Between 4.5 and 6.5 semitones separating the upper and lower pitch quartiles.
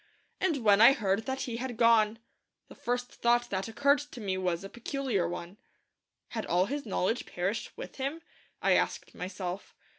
Yes: average, 5.2 semitones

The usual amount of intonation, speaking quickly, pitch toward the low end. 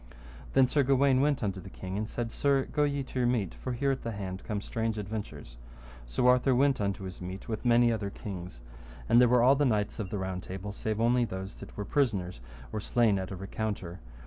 Yes: average, 4.6 semitones; fast, 225 wpm; low, 110 Hz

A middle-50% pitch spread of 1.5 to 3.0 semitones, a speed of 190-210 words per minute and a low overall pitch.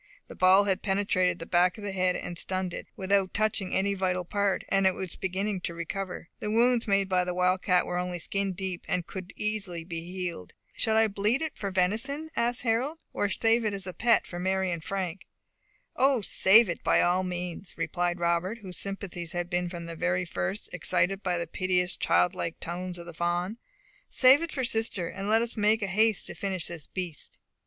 No: narrow, 2.6 semitones; average, 200 wpm; high, 190 Hz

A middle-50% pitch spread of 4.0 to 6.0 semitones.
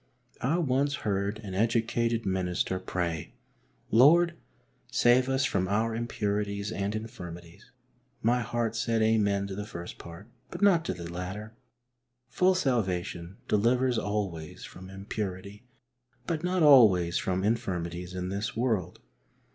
Yes: average, 4.4 semitones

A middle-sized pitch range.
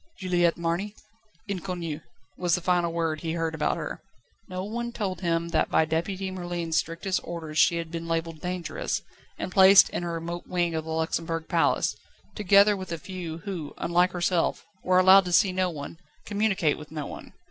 No: narrow, 2.1 semitones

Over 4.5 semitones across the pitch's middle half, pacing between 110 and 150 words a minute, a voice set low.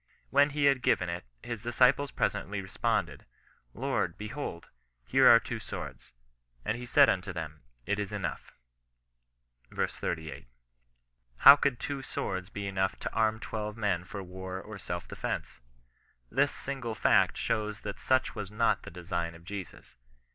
No: average, 4.9 semitones; average, 160 wpm; low, 105 Hz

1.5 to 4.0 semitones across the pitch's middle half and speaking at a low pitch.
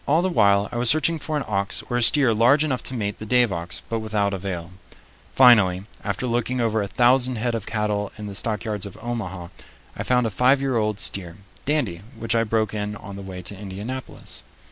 Yes: average, 3.7 semitones; low, 110 Hz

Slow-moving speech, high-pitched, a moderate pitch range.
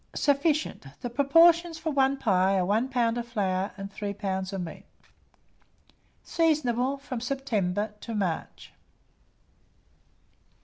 No: slow, 120 wpm; high, 235 Hz; wide, 5.9 semitones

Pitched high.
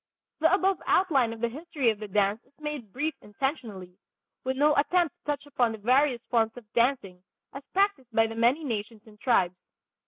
Yes: high, 245 Hz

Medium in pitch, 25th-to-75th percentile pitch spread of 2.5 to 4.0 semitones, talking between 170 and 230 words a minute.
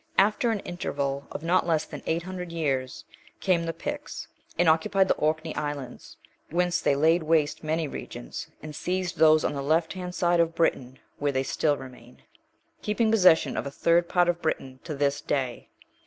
Yes: medium, 160 Hz; average, 3.6 semitones; average, 185 wpm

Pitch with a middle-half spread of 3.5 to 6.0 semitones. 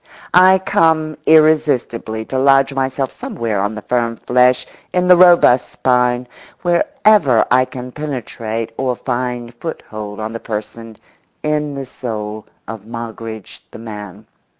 Yes: average, 4.7 semitones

